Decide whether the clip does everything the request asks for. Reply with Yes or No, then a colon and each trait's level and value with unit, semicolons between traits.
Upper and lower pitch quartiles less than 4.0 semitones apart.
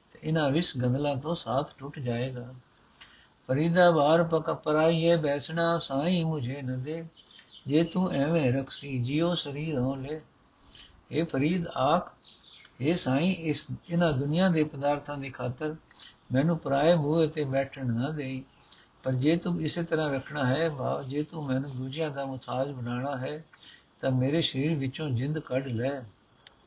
Yes: average, 3.5 semitones